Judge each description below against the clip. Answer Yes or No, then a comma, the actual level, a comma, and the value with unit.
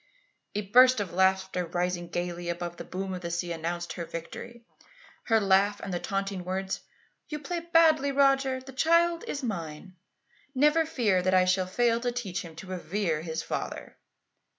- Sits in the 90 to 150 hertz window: No, high, 190 Hz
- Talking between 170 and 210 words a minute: Yes, average, 175 wpm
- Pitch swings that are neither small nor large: No, wide, 6.5 semitones